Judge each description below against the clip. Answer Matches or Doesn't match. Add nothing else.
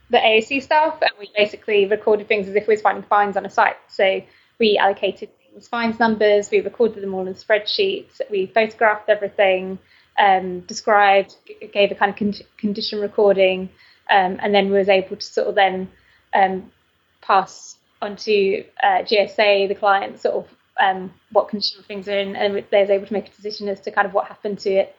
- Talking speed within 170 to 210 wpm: Matches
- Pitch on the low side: Doesn't match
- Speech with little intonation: Matches